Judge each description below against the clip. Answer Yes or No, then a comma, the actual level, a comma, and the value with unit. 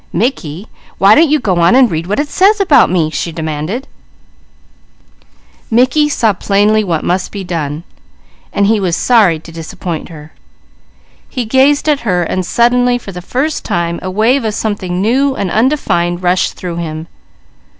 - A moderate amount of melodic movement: No, wide, 6.3 semitones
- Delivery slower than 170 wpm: Yes, average, 140 wpm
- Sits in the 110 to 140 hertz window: No, high, 200 Hz